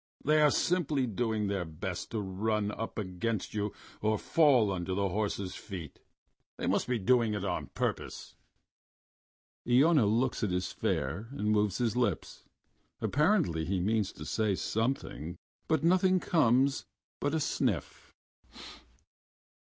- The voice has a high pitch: No, low, 110 Hz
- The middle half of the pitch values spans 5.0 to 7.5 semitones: Yes, average, 5.3 semitones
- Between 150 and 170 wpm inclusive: No, slow, 135 wpm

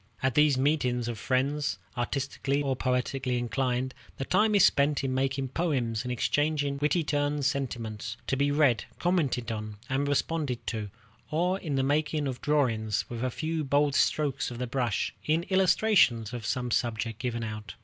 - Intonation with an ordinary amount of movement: Yes, average, 3.5 semitones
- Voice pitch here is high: No, low, 135 Hz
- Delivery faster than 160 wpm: Yes, average, 170 wpm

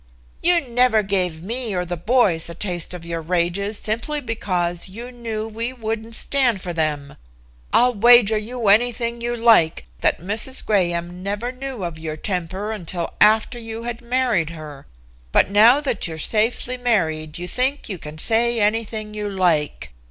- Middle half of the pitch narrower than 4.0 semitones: No, wide, 5.4 semitones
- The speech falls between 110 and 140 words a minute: No, average, 165 wpm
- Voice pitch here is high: Yes, high, 210 Hz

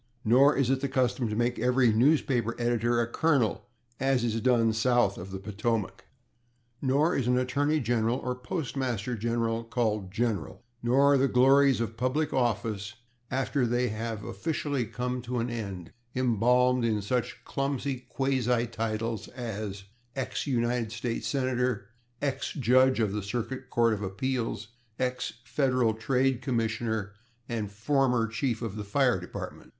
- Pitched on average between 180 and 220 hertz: No, low, 120 Hz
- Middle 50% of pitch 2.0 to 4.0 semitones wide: Yes, narrow, 2.6 semitones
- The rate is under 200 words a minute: Yes, average, 150 wpm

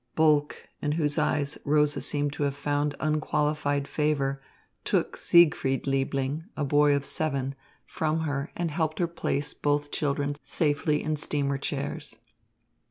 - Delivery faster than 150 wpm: No, average, 145 wpm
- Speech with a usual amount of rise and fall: No, narrow, 1.3 semitones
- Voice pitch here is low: No, medium, 145 Hz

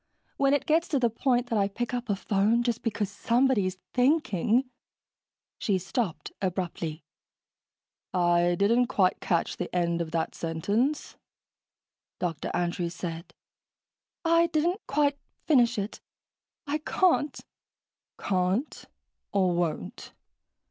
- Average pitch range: No, wide, 6.7 semitones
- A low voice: No, high, 205 Hz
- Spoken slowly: Yes, slow, 120 wpm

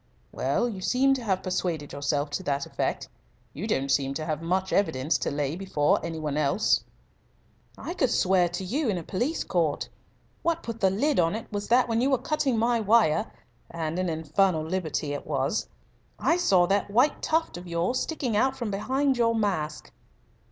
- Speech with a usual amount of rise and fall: No, wide, 6.9 semitones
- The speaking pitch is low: No, high, 190 Hz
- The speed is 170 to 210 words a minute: Yes, average, 190 wpm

